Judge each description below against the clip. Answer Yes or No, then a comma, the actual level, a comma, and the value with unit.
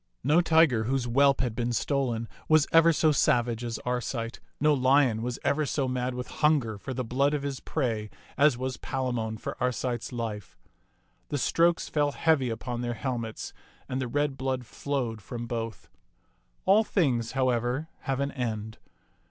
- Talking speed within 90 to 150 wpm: No, average, 165 wpm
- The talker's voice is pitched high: No, low, 130 Hz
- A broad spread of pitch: No, average, 3.2 semitones